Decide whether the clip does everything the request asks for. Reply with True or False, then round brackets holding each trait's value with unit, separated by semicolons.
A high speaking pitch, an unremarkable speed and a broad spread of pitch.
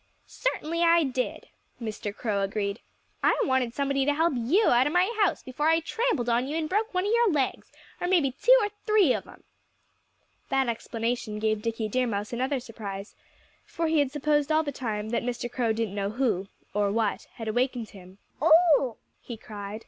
True (255 Hz; 190 wpm; 6.1 semitones)